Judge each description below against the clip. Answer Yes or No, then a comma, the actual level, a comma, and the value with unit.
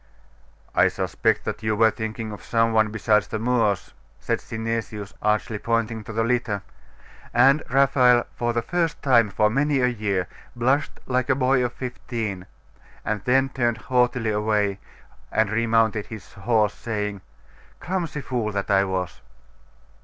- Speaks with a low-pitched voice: Yes, low, 115 Hz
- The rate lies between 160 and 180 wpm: No, average, 150 wpm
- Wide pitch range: No, average, 2.8 semitones